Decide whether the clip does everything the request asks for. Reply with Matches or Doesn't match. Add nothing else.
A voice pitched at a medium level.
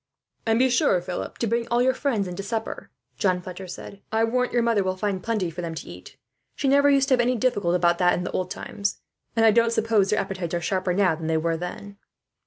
Doesn't match